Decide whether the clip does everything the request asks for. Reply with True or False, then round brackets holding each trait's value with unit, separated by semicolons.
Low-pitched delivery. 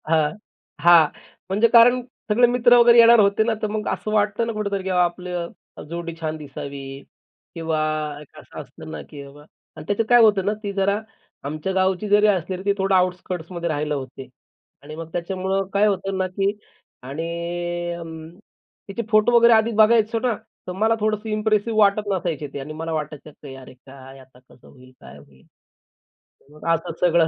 False (185 Hz)